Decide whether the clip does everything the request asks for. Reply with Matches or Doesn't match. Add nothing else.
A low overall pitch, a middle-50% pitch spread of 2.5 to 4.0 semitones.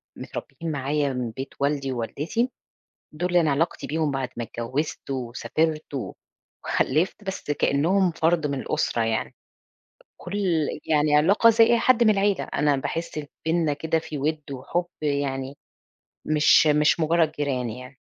Doesn't match